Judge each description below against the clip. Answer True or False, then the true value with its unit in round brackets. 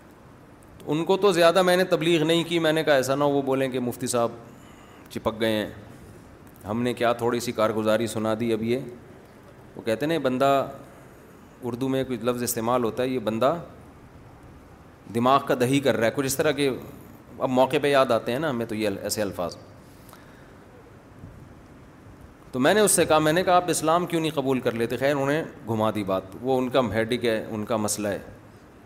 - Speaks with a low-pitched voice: True (125 Hz)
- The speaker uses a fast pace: True (210 wpm)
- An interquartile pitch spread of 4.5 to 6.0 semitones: False (4.1 semitones)